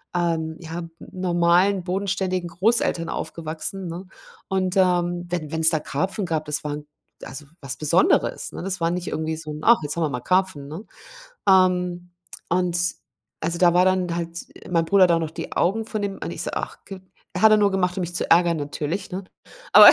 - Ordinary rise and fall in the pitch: No, narrow, 2.3 semitones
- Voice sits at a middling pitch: Yes, medium, 175 Hz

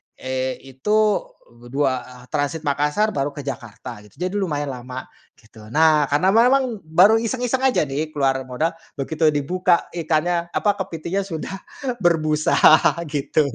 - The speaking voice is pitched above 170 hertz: No, medium, 155 Hz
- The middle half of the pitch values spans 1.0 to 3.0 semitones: No, average, 5.2 semitones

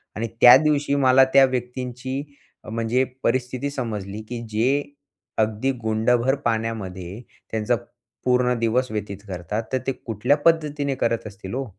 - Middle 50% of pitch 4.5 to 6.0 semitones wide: No, average, 3.2 semitones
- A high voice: No, low, 120 Hz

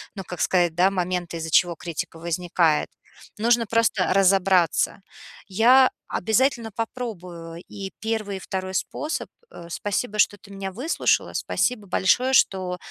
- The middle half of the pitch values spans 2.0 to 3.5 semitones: No, average, 3.9 semitones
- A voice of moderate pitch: No, high, 195 Hz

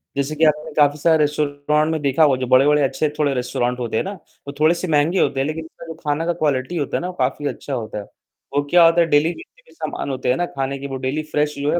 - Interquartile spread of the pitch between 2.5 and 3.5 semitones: Yes, average, 2.8 semitones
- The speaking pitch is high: No, medium, 150 Hz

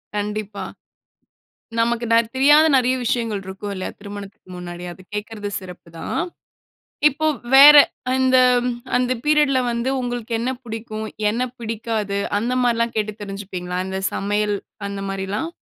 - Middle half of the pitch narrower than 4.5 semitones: Yes, average, 3.6 semitones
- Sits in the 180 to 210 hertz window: No, high, 220 Hz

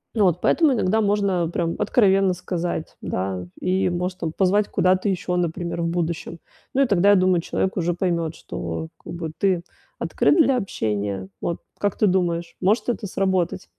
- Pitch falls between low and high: Yes, medium, 180 Hz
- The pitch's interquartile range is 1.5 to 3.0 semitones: Yes, narrow, 2.6 semitones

